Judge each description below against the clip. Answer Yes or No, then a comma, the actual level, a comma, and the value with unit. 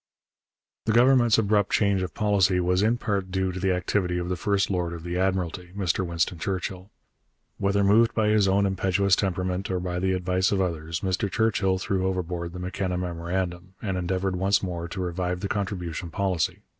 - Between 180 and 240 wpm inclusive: Yes, average, 185 wpm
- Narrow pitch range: Yes, narrow, 1.8 semitones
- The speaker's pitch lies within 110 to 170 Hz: No, very low, 95 Hz